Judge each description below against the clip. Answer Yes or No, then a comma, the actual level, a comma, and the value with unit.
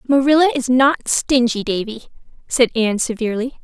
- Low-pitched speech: No, high, 245 Hz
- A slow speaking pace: Yes, slow, 130 wpm